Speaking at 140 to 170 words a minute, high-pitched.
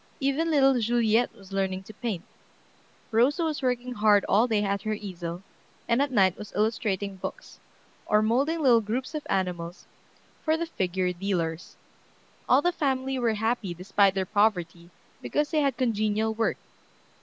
Yes: average, 155 wpm; high, 215 Hz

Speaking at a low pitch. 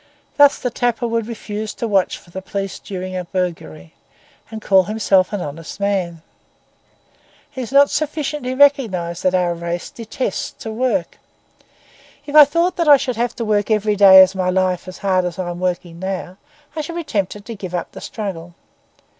No: high, 200 Hz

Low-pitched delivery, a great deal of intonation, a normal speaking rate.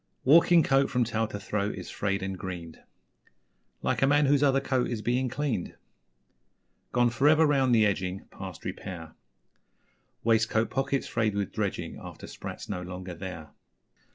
Yes: low, 110 Hz; wide, 6.0 semitones; average, 155 wpm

